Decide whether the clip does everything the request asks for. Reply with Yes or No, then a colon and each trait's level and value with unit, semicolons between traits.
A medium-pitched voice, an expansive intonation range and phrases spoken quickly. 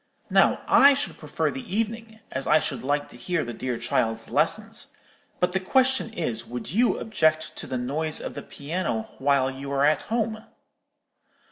No: medium, 155 Hz; wide, 8.6 semitones; average, 175 wpm